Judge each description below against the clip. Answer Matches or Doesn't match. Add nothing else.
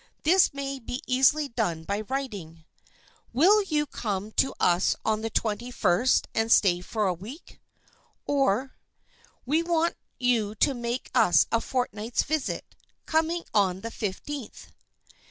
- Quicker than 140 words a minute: Doesn't match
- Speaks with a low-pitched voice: Doesn't match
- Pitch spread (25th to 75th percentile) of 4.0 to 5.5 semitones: Matches